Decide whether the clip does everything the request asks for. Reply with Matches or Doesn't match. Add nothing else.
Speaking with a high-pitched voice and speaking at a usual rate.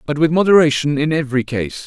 Doesn't match